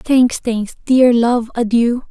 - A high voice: Yes, high, 240 Hz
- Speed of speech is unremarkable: Yes, average, 145 wpm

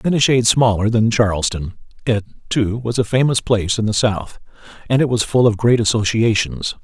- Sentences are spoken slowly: No, average, 195 wpm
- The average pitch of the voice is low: Yes, low, 110 Hz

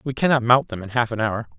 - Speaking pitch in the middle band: No, low, 120 Hz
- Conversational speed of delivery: No, fast, 265 wpm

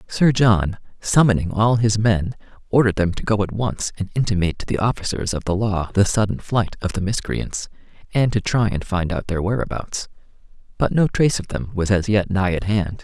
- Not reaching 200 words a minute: No, fast, 205 wpm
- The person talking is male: Yes, male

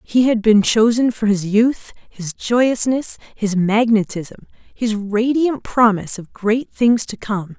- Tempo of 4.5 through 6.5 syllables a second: No, 3.8 syllables/s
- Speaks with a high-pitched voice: Yes, high, 220 Hz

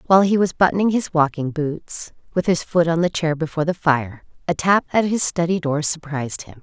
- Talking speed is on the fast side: Yes, fast, 215 wpm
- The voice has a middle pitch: Yes, medium, 165 Hz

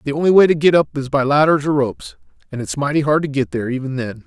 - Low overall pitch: No, medium, 145 Hz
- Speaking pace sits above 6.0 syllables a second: Yes, 7.2 syllables/s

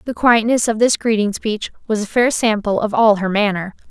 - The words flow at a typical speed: No, fast, 215 wpm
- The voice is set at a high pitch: Yes, high, 215 Hz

